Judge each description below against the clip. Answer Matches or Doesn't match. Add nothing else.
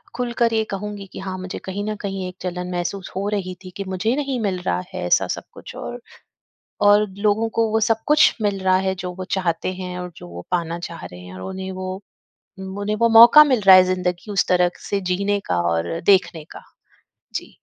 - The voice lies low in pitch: Doesn't match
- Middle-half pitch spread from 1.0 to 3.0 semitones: Matches